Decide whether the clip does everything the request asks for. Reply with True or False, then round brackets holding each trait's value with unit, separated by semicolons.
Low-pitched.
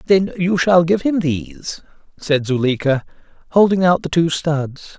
False (165 Hz)